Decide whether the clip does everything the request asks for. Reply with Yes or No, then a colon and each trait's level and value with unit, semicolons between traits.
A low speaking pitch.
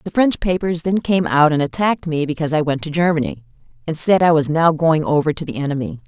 No: medium, 160 Hz